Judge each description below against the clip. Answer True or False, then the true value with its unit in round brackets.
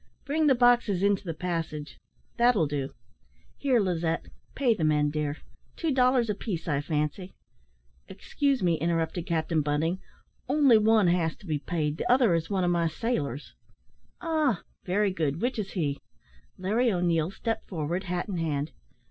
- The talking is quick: False (165 wpm)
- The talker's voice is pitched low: False (175 Hz)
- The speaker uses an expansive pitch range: True (6.3 semitones)